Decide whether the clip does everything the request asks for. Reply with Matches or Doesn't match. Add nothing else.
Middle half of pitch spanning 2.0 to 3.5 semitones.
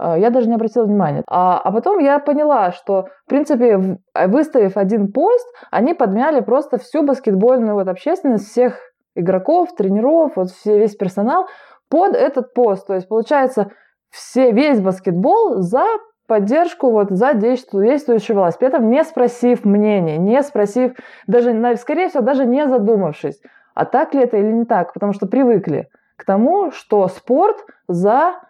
Doesn't match